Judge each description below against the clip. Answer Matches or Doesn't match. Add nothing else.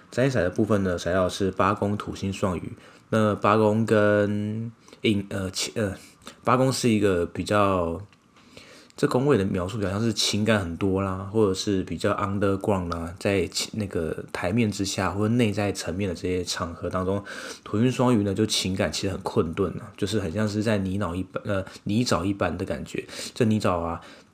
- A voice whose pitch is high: Doesn't match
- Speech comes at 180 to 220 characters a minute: Doesn't match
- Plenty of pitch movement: Doesn't match